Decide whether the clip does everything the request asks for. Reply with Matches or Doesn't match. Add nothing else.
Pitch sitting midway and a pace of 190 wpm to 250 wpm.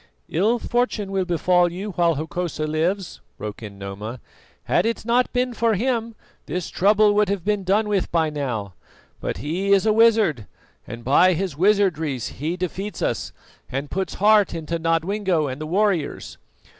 Doesn't match